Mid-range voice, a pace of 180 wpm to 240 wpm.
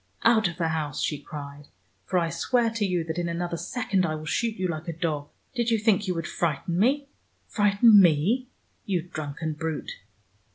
Yes: medium, 175 Hz; average, 195 wpm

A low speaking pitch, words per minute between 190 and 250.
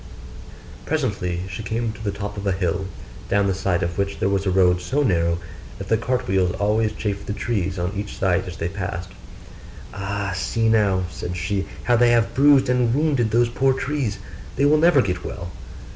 Yes: low, 100 Hz; average, 200 wpm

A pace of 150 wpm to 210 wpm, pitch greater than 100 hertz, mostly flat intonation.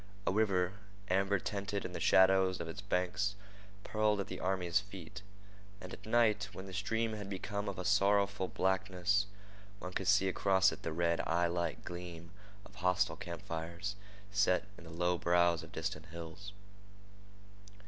No: average, 160 wpm; very low, 95 Hz; narrow, 2.3 semitones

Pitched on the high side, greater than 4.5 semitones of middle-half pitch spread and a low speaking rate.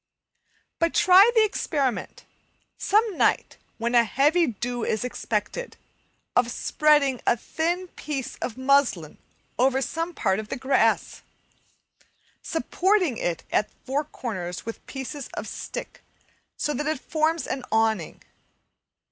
Yes: very high, 270 Hz; wide, 5.5 semitones; slow, 130 wpm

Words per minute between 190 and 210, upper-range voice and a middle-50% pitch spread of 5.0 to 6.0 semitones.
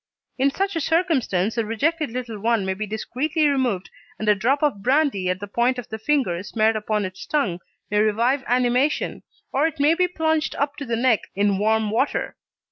Yes: average, 200 wpm; high, 240 Hz; average, 5.3 semitones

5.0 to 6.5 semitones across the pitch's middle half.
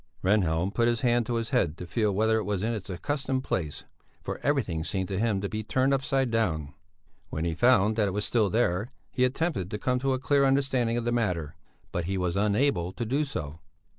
Yes: average, 5.3 semitones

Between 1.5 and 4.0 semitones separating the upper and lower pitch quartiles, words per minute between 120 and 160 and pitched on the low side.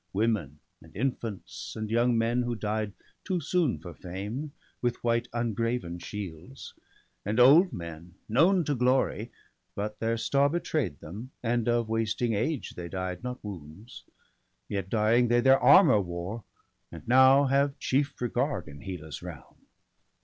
No: average, 4.7 semitones; average, 145 wpm; low, 115 Hz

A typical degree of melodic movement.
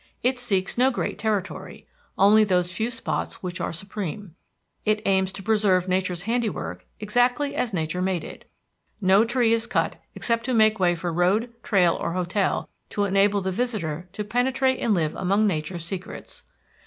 Yes: average, 3.8 semitones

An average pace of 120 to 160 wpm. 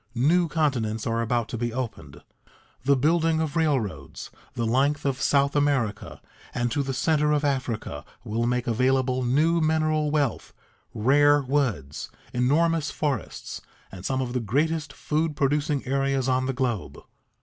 Yes: average, 150 wpm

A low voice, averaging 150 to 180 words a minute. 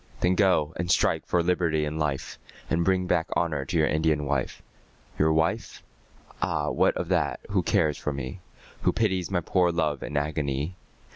Yes: very low, 80 Hz; average, 175 wpm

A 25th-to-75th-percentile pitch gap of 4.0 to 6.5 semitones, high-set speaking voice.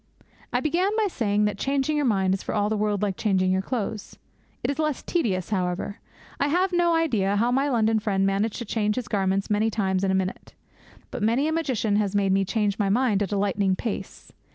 Yes: average, 4.6 semitones; high, 210 Hz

